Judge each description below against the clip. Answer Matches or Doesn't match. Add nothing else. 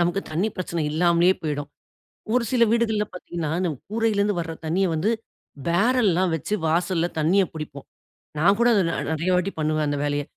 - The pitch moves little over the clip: Doesn't match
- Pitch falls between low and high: Matches